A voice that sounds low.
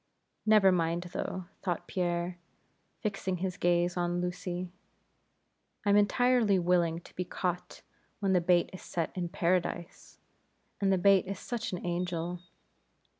No: medium, 180 Hz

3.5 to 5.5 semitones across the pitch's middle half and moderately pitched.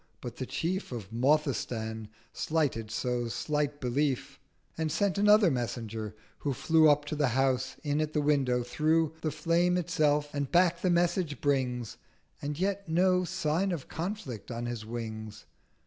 Yes: average, 5.2 semitones; medium, 145 Hz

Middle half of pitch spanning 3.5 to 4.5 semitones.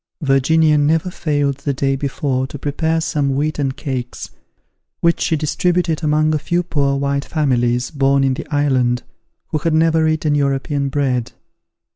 No: narrow, 2.5 semitones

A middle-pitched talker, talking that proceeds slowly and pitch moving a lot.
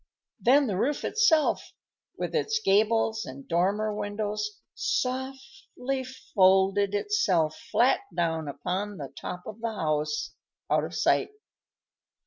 No: high, 210 Hz; slow, 115 wpm; wide, 6.2 semitones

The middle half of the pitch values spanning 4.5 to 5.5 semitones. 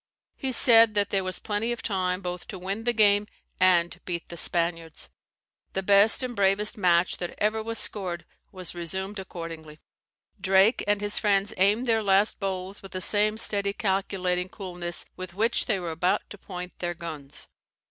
No: average, 2.7 semitones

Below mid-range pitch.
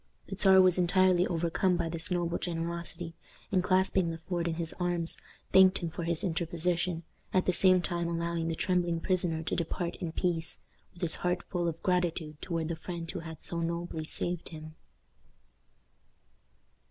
No: medium, 170 Hz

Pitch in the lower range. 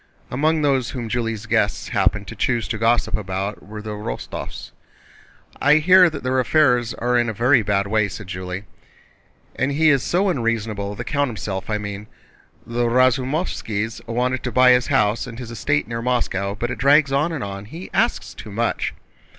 Yes: low, 120 Hz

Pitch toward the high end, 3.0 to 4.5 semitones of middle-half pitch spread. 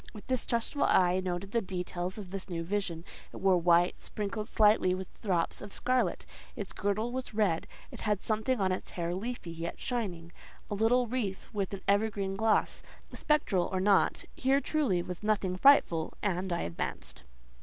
Yes: high, 195 Hz; average, 3.5 semitones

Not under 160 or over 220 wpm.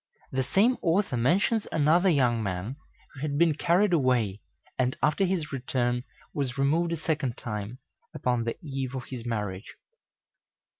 No: average, 150 wpm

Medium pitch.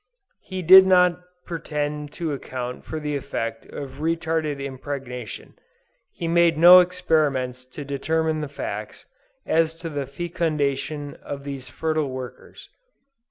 Yes: medium, 150 Hz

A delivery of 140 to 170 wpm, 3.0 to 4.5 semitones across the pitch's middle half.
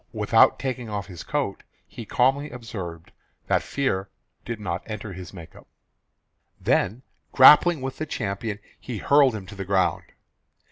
No: average, 150 wpm; average, 5.2 semitones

